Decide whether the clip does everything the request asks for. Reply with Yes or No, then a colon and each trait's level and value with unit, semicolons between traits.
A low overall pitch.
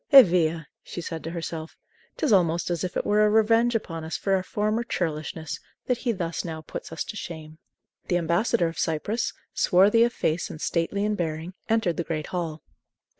No: medium, 175 Hz